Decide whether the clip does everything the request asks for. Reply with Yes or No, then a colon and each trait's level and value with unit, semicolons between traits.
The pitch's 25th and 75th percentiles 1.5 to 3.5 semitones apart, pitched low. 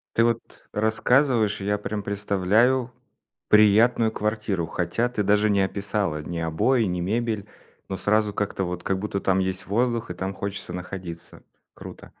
Yes: average, 2.7 semitones; low, 105 Hz